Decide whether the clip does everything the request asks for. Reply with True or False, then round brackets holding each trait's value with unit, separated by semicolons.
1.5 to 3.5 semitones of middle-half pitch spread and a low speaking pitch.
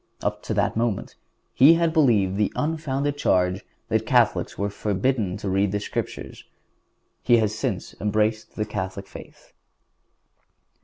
False (5.1 semitones; 105 Hz)